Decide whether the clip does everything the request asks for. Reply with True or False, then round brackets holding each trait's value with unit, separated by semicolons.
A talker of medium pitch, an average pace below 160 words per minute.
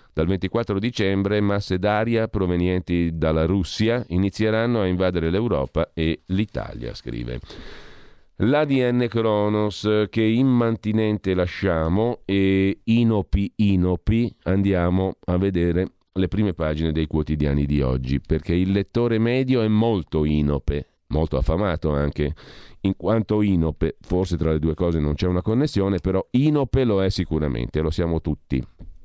False (95 Hz; 130 wpm)